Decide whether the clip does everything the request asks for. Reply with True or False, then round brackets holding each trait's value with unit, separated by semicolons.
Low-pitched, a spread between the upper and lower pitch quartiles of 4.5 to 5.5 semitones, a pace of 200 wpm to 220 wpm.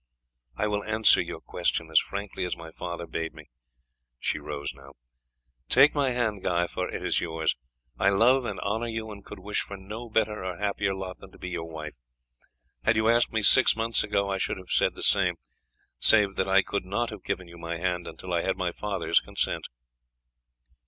False (100 Hz; 3.7 semitones; 205 wpm)